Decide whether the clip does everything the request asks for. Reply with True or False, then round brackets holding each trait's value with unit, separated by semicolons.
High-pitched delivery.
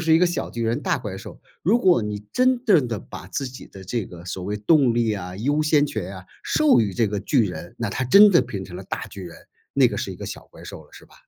False (115 Hz)